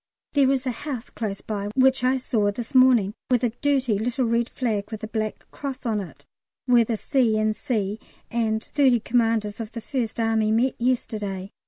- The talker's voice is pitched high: Yes, high, 230 Hz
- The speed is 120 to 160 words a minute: No, average, 190 wpm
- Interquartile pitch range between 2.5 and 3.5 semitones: Yes, average, 2.9 semitones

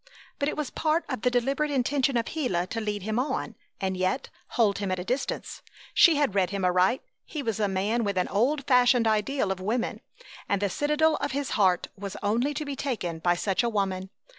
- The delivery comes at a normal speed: No, fast, 215 wpm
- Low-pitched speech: No, high, 225 Hz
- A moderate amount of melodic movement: No, wide, 6.1 semitones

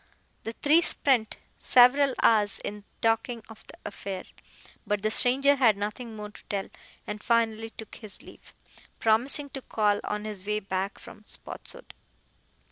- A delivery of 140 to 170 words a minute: Yes, average, 150 wpm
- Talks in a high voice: Yes, high, 220 Hz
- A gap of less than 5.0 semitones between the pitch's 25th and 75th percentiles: Yes, average, 3.0 semitones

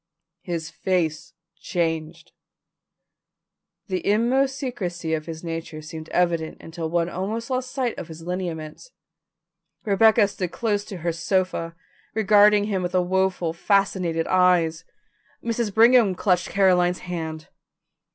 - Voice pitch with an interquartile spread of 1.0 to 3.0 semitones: No, average, 3.8 semitones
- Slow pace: Yes, slow, 120 wpm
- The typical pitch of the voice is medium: Yes, medium, 180 Hz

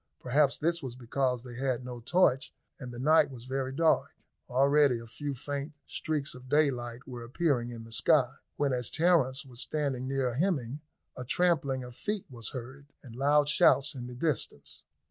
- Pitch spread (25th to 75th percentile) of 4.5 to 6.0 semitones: No, average, 2.9 semitones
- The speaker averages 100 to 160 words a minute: No, average, 180 wpm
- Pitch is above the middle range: No, low, 130 Hz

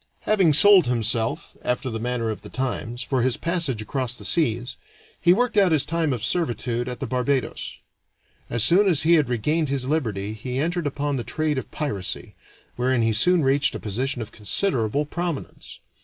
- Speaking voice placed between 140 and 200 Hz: No, low, 130 Hz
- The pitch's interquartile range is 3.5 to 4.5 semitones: No, average, 5.1 semitones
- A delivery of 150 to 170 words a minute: No, average, 185 wpm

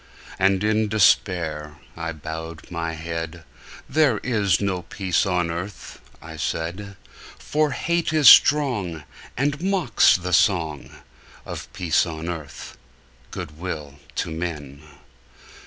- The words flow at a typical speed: No, slow, 120 wpm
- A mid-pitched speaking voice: No, very low, 90 Hz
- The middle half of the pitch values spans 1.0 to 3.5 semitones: No, average, 4.5 semitones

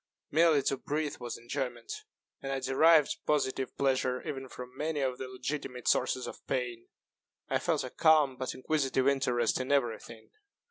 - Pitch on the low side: Yes, low, 130 Hz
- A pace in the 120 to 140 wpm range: No, average, 160 wpm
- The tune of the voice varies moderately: No, narrow, 2.3 semitones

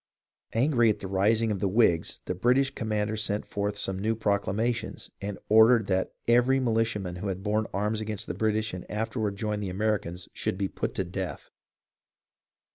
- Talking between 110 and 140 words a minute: No, average, 180 wpm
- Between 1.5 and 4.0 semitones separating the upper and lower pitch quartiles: Yes, narrow, 2.5 semitones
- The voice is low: Yes, low, 105 Hz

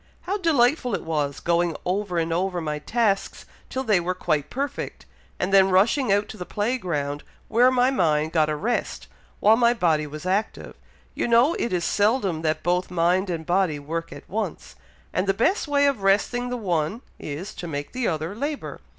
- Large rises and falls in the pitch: Yes, wide, 6.3 semitones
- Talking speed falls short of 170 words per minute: No, average, 195 wpm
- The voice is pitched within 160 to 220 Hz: Yes, high, 190 Hz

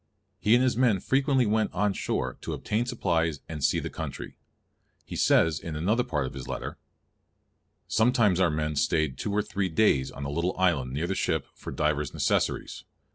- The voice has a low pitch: Yes, very low, 90 Hz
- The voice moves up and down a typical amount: No, wide, 6.3 semitones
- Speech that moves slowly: No, average, 185 wpm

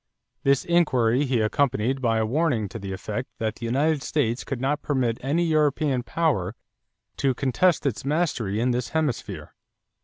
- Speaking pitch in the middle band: No, low, 130 Hz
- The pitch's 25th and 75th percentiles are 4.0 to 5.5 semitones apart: Yes, average, 4.5 semitones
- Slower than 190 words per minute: Yes, average, 160 wpm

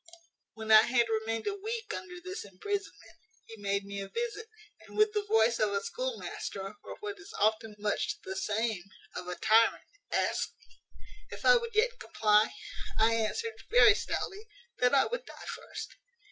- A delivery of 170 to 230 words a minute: Yes, average, 175 wpm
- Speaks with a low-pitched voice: No, high, 230 Hz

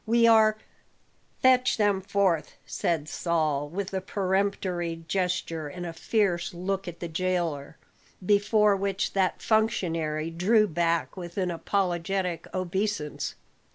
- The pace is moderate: No, slow, 125 wpm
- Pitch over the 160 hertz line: Yes, medium, 185 Hz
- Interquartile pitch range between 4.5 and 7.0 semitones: No, average, 3.1 semitones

